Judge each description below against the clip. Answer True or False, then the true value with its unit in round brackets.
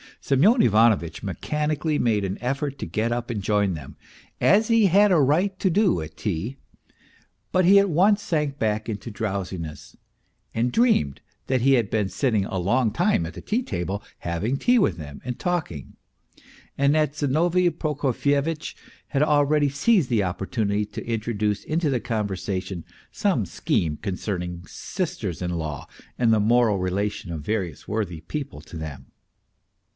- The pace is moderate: True (160 wpm)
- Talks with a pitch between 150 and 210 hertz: False (115 Hz)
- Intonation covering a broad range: True (7.8 semitones)